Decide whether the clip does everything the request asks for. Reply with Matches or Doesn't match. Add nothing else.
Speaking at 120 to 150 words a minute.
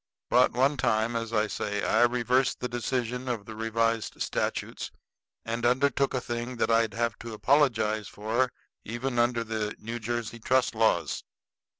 Doesn't match